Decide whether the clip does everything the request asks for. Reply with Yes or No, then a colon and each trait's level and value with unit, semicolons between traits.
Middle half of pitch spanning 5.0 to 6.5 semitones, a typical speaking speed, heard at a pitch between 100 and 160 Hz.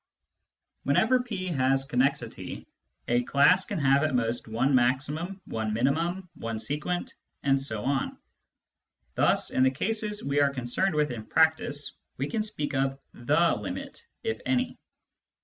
Yes: wide, 5.5 semitones; average, 145 wpm; medium, 140 Hz